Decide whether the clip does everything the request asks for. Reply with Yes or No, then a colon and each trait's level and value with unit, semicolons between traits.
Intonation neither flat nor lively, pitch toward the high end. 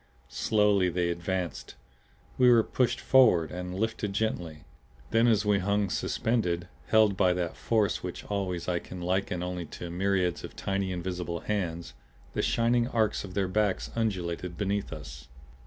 No: average, 3.1 semitones; very low, 95 Hz